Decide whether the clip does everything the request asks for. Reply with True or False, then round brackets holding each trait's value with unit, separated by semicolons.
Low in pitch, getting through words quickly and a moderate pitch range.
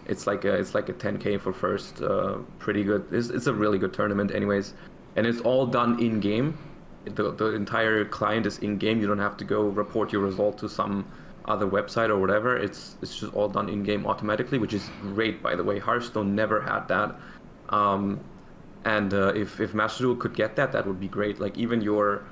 False (105 Hz; 215 wpm; 1.5 semitones)